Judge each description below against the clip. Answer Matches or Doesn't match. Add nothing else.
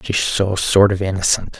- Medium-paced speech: Matches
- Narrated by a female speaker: Doesn't match